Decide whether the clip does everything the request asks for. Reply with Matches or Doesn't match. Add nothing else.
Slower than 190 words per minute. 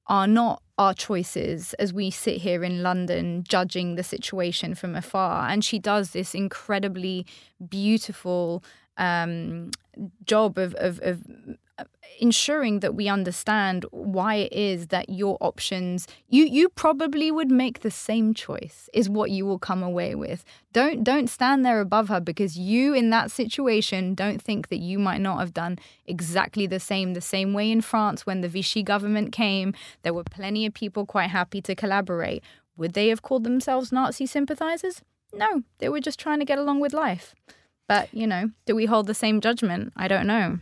Matches